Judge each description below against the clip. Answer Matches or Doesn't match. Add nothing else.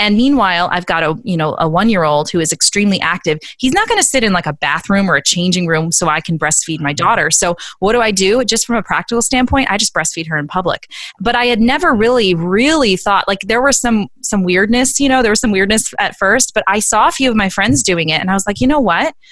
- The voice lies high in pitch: Matches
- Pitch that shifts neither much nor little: Doesn't match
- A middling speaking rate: Doesn't match